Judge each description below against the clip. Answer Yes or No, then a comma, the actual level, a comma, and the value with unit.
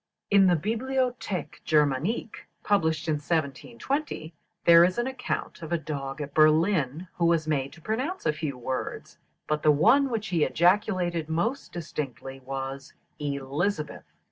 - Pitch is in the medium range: Yes, medium, 160 Hz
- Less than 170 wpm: Yes, average, 145 wpm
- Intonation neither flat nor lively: No, wide, 5.7 semitones